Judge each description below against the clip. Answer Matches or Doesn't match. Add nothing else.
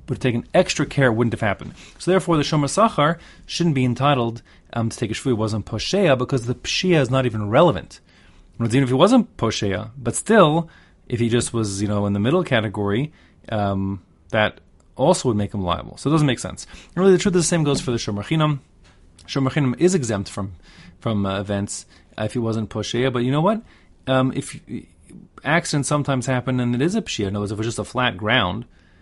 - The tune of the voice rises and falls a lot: Matches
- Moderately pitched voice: Doesn't match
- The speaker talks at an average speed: Doesn't match